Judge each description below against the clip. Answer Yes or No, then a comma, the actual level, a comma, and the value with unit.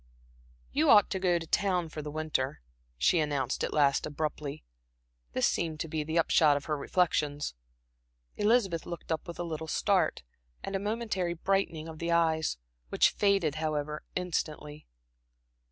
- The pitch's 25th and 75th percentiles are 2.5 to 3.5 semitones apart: Yes, average, 3.0 semitones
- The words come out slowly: No, average, 155 wpm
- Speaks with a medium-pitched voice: Yes, medium, 160 Hz